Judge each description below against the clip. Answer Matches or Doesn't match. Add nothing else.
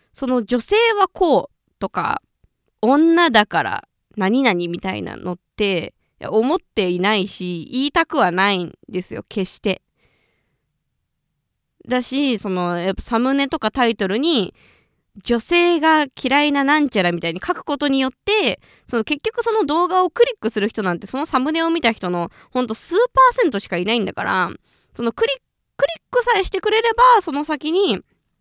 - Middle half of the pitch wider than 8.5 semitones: Matches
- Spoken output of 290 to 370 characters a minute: Matches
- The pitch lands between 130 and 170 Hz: Doesn't match